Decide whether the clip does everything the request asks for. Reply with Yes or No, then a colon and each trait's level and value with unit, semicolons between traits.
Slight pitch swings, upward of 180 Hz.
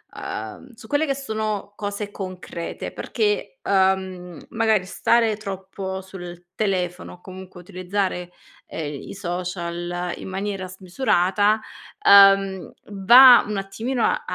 No: average, 3.0 semitones; high, 190 Hz